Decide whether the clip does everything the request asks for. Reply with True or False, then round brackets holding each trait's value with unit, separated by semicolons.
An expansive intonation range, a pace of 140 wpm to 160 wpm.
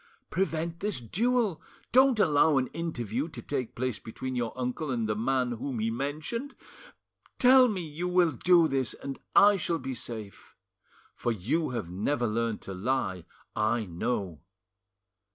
True (6.7 semitones; 150 wpm)